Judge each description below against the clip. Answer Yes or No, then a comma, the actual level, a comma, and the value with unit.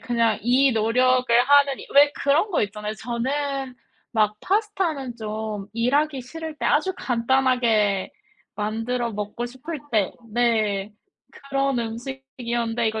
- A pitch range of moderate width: Yes, average, 3.8 semitones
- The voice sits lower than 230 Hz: No, high, 245 Hz